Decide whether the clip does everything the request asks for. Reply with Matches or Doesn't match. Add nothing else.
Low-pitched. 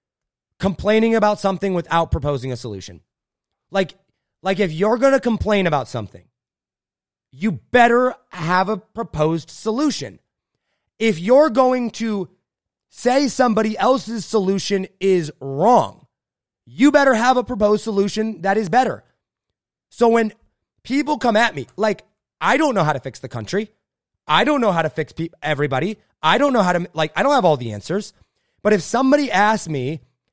Doesn't match